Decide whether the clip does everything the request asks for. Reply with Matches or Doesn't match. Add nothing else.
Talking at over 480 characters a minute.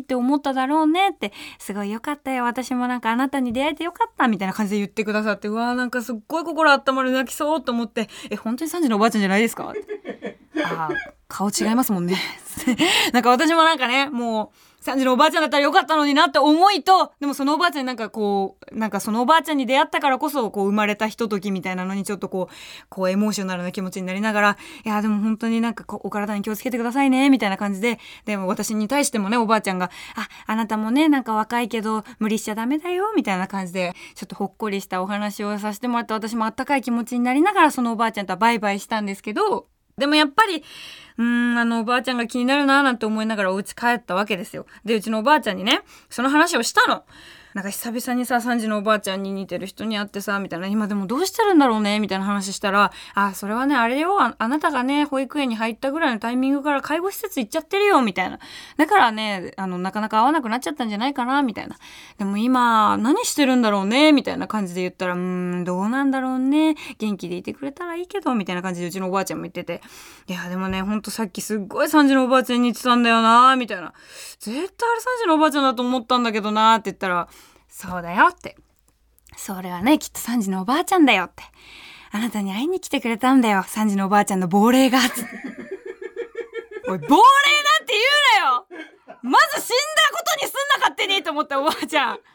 Matches